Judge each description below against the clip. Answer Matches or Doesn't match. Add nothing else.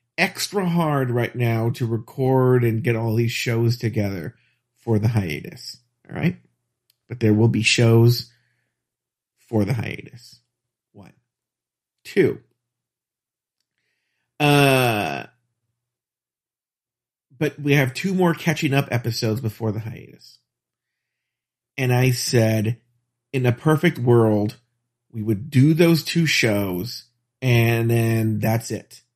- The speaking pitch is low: Matches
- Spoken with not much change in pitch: Matches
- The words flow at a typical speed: Doesn't match